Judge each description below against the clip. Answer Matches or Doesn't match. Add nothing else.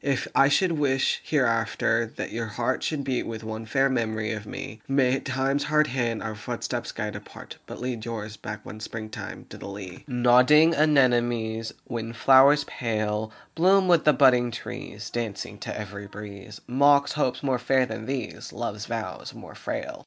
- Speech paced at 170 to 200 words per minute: Matches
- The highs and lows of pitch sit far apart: Doesn't match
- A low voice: Matches